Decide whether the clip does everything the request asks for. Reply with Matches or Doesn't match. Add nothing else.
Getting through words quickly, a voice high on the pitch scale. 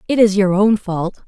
Matches